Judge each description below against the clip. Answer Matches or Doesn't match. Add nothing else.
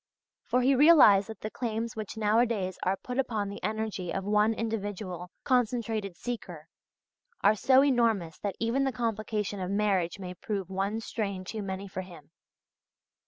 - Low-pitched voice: Doesn't match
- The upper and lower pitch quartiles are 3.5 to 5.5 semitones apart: Doesn't match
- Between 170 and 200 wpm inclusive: Doesn't match